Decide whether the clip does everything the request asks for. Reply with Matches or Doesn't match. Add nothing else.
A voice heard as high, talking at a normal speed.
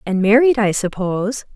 Matches